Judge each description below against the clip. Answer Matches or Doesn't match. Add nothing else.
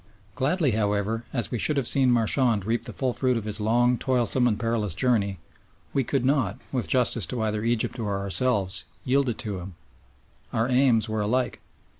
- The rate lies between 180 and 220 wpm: Matches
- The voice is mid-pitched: Doesn't match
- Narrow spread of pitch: Doesn't match